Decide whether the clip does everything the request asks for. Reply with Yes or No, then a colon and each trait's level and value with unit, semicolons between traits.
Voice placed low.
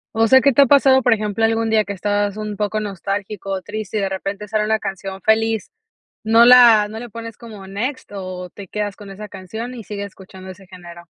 No: high, 210 Hz